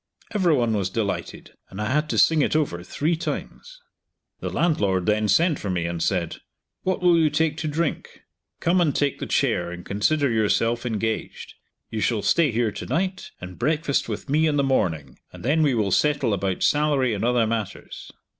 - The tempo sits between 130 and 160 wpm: No, average, 190 wpm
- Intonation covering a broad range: Yes, wide, 7.1 semitones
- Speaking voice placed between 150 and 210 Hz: No, low, 125 Hz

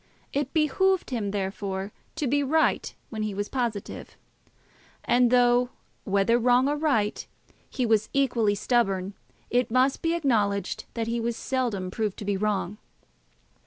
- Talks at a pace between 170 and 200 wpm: No, average, 145 wpm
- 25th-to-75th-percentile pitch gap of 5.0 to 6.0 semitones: No, average, 4.2 semitones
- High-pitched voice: Yes, high, 235 Hz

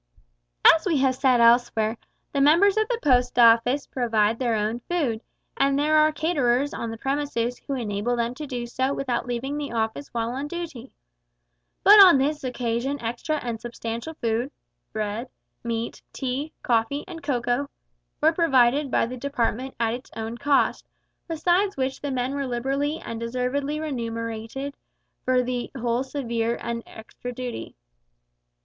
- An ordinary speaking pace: Yes, average, 155 wpm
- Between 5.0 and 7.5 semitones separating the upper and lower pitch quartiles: No, average, 3.4 semitones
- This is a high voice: Yes, very high, 255 Hz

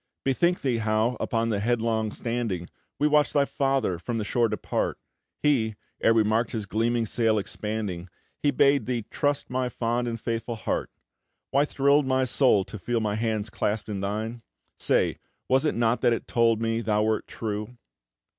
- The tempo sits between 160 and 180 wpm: Yes, average, 175 wpm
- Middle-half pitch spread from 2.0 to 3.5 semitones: Yes, average, 2.7 semitones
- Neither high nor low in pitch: No, low, 115 Hz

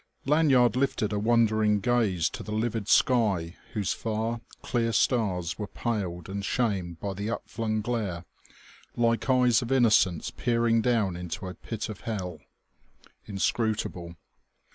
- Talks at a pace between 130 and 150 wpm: Yes, average, 140 wpm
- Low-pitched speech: Yes, low, 110 Hz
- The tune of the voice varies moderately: Yes, average, 3.4 semitones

